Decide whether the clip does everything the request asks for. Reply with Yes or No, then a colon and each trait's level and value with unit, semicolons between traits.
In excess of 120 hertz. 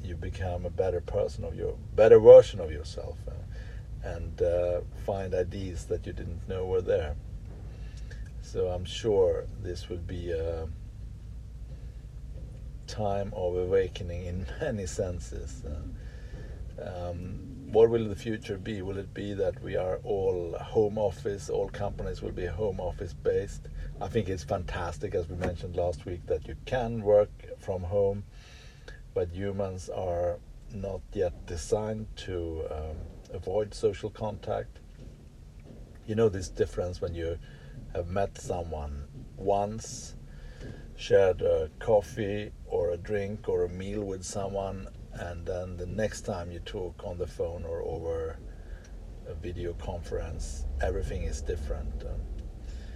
No: very low, 95 Hz